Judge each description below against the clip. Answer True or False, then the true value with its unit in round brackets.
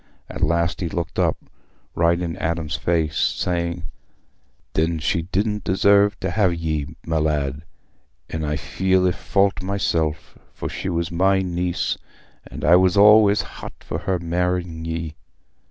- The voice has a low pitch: True (85 Hz)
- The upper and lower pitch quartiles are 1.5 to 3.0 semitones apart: True (2.6 semitones)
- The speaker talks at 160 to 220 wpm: False (150 wpm)